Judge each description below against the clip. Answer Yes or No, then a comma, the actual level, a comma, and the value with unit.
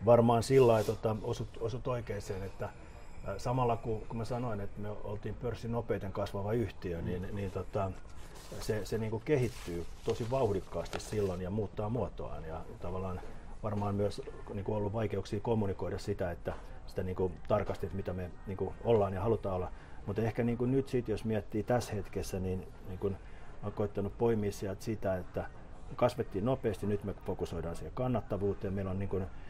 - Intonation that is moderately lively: Yes, average, 3.2 semitones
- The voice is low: Yes, low, 100 Hz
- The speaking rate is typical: No, fast, 180 wpm